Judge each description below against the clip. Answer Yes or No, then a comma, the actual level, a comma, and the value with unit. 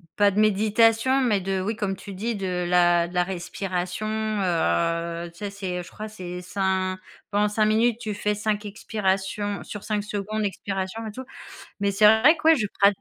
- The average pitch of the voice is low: No, high, 205 Hz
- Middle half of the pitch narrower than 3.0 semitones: Yes, narrow, 2.5 semitones